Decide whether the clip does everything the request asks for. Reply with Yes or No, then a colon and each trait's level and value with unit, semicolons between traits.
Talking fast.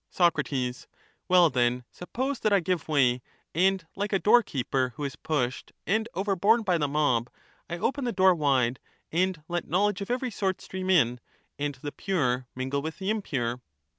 No: average, 170 wpm